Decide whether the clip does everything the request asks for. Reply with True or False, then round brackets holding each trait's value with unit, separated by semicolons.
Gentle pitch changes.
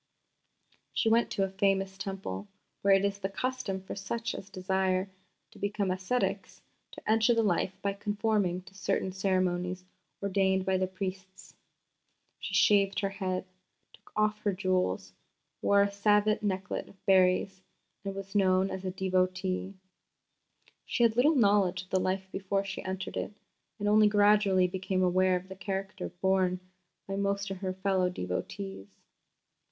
True (1.3 semitones)